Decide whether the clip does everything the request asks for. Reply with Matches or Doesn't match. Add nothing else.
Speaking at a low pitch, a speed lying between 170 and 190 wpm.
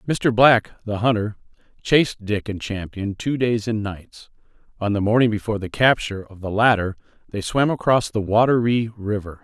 Matches